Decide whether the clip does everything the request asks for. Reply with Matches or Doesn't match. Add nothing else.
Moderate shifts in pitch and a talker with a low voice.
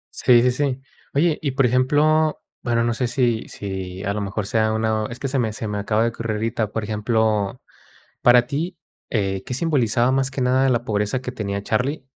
Matches